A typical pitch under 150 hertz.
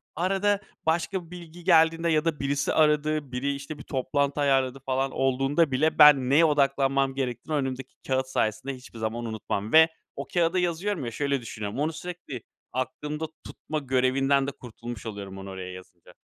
Yes: medium, 140 Hz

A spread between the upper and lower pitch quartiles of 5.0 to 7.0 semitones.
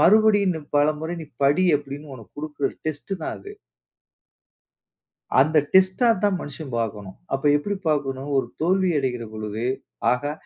Yes: wide, 5.4 semitones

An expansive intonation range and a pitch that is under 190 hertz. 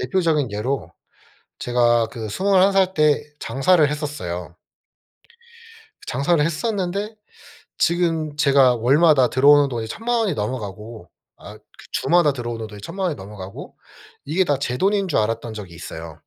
Yes: wide, 7.2 semitones; medium, 140 Hz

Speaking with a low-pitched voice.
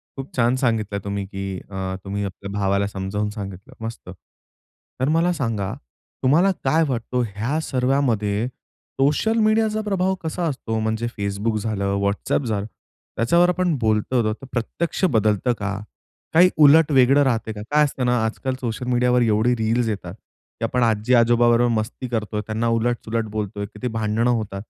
Yes: low, 115 Hz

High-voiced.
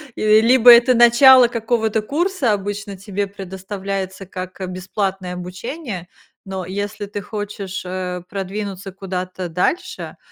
Yes: high, 200 Hz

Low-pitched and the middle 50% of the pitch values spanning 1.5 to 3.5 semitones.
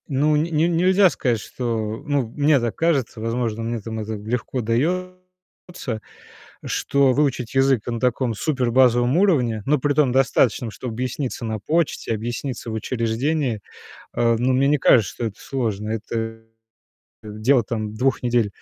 No: low, 125 Hz; average, 4.1 semitones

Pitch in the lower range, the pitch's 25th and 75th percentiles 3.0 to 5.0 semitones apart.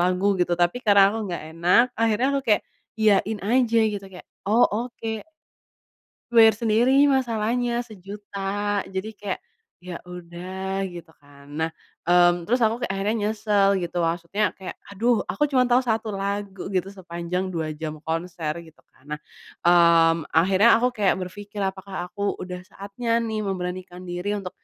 No: high, 195 Hz; average, 3.7 semitones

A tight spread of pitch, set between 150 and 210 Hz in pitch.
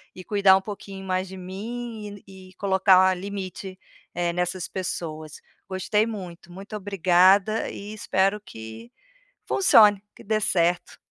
Yes: narrow, 2.1 semitones; high, 190 Hz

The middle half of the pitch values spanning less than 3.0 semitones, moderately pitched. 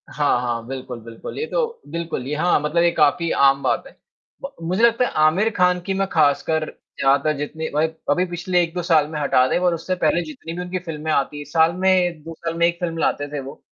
No: average, 3.4 semitones; medium, 165 Hz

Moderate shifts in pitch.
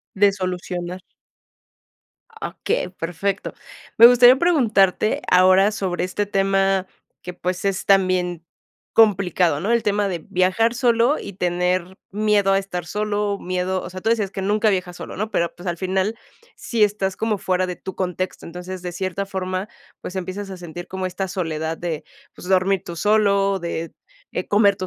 No: narrow, 2.2 semitones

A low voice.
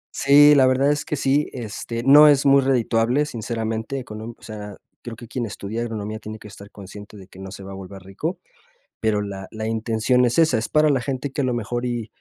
Yes: low, 115 Hz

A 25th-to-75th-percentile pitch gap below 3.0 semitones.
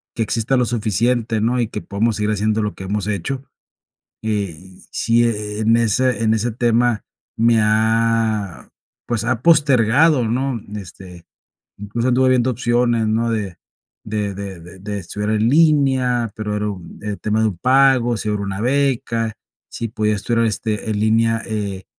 Yes: narrow, 2.4 semitones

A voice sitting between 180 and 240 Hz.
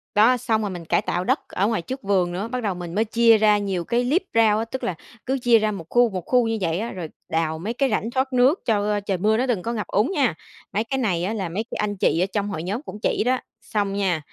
Yes: high, 215 Hz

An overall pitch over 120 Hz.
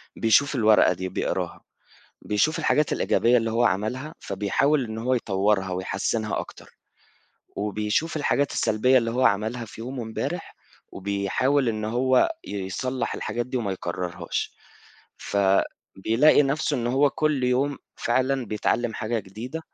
No: low, 115 Hz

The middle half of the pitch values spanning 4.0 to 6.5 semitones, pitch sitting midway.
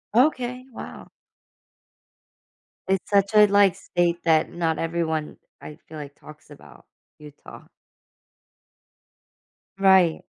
Yes: average, 4.3 semitones; medium, 170 Hz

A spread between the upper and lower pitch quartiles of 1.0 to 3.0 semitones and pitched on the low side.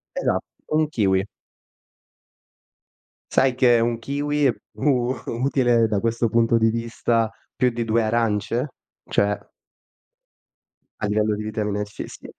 Yes: narrow, 2.5 semitones; low, 115 Hz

